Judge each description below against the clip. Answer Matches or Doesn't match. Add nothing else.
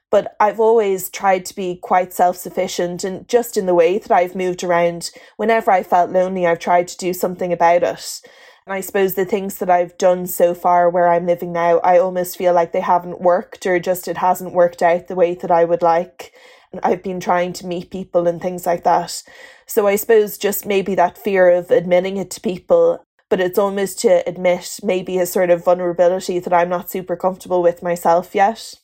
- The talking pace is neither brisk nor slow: Doesn't match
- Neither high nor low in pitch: Matches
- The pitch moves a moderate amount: Doesn't match